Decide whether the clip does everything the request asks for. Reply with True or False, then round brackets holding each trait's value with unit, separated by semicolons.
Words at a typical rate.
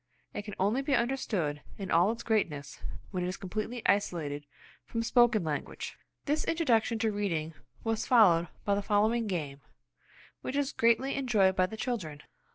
True (165 wpm)